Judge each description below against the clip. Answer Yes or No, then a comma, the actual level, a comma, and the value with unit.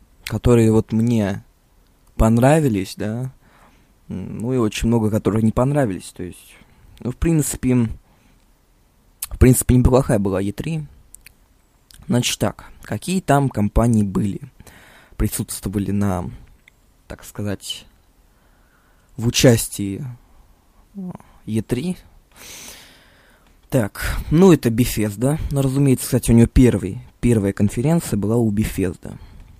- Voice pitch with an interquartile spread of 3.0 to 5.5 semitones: Yes, average, 4.0 semitones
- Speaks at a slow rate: Yes, slow, 100 wpm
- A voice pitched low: Yes, low, 115 Hz